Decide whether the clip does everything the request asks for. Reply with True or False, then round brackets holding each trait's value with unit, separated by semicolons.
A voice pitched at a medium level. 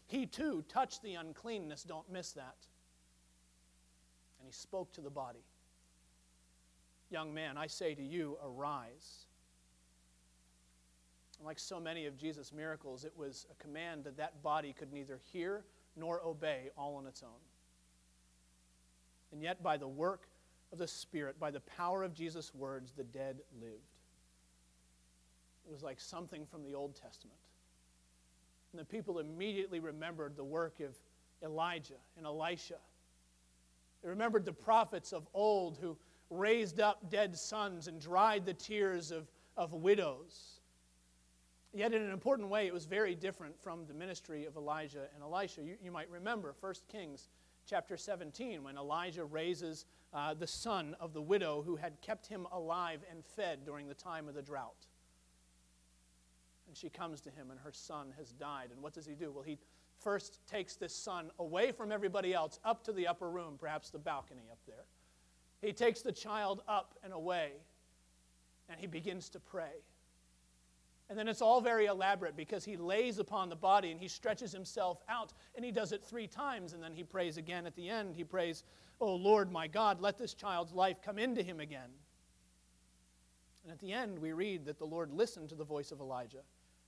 True (155 Hz)